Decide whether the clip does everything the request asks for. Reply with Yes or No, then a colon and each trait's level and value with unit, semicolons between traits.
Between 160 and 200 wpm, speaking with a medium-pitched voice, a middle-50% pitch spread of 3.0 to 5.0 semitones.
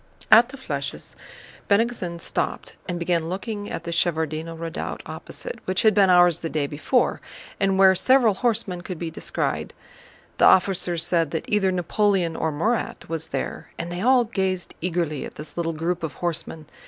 Yes: average, 170 wpm; medium, 175 Hz; average, 3.6 semitones